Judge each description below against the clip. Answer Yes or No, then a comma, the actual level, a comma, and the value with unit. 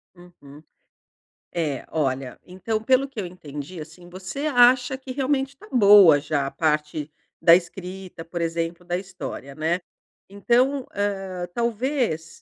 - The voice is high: No, medium, 180 Hz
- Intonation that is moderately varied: No, wide, 6.7 semitones